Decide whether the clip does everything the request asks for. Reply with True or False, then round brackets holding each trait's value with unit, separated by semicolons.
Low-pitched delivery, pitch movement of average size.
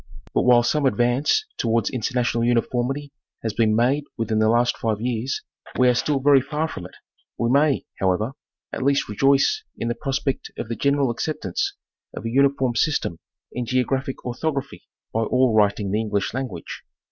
True (125 Hz; 3.3 semitones)